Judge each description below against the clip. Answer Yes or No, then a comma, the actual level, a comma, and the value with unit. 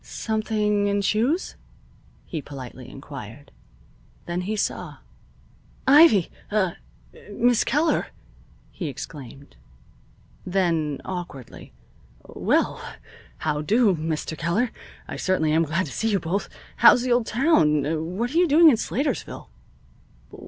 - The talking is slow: Yes, slow, 115 wpm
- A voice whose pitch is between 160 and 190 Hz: Yes, medium, 185 Hz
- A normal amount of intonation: No, wide, 6.7 semitones